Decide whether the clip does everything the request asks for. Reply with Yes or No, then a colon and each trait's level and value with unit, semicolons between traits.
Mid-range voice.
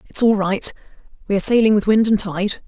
No: high, 205 Hz